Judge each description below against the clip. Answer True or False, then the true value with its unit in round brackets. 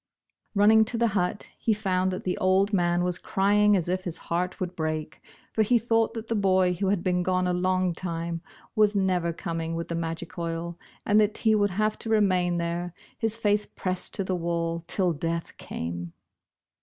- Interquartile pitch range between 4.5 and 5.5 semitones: False (3.3 semitones)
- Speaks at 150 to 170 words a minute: False (195 wpm)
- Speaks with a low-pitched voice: False (185 Hz)